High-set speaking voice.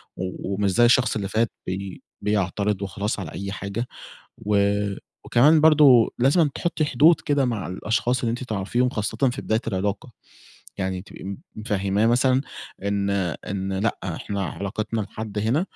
No: low, 105 Hz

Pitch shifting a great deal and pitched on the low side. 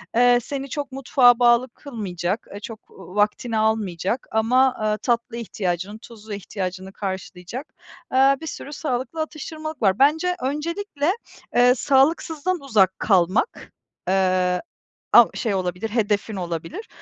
No: wide, 6.1 semitones; high, 230 Hz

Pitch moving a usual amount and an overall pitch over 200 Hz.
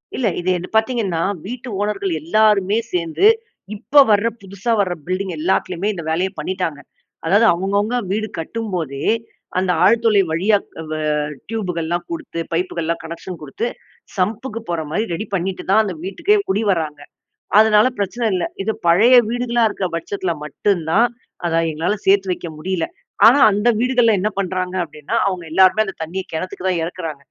No: average, 4.0 semitones; high, 190 Hz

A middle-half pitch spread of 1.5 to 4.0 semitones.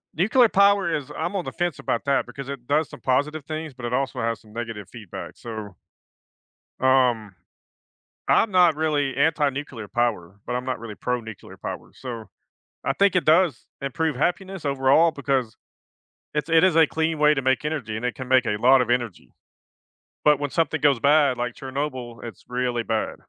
No: average, 4.5 semitones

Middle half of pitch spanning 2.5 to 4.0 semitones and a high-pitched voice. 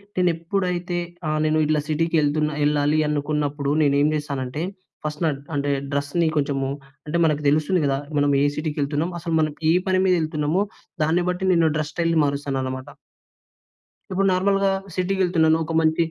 No: average, 2.9 semitones; medium, 155 Hz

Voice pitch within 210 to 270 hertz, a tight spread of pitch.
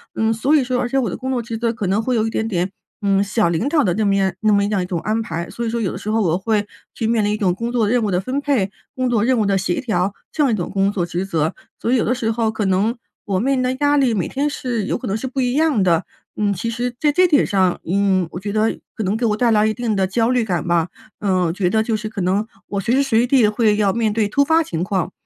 No: high, 215 Hz; average, 3.8 semitones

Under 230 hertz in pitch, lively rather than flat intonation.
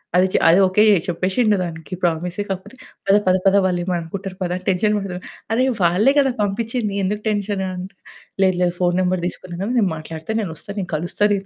No: medium, 185 Hz; narrow, 2.6 semitones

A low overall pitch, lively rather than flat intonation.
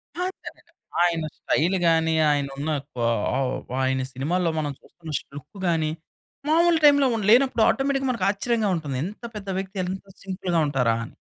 No: medium, 180 Hz; wide, 6.8 semitones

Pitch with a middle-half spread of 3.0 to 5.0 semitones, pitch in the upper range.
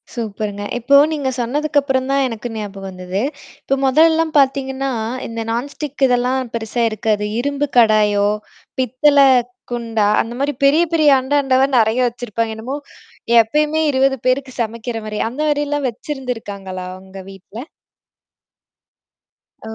Yes: average, 4.0 semitones; very high, 250 Hz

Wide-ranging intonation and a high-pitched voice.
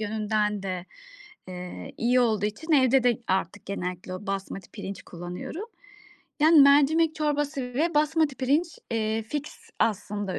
Yes: wide, 6.8 semitones; high, 225 Hz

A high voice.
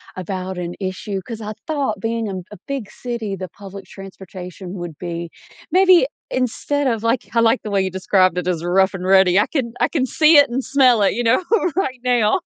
Yes: high, 210 Hz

